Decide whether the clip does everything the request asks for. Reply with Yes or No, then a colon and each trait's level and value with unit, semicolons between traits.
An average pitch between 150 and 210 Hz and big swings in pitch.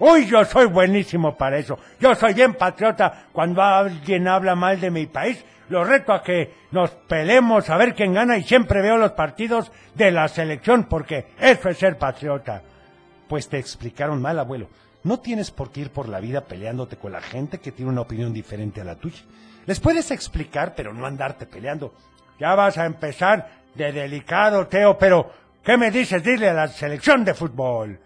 Yes: medium, 165 Hz; wide, 7.3 semitones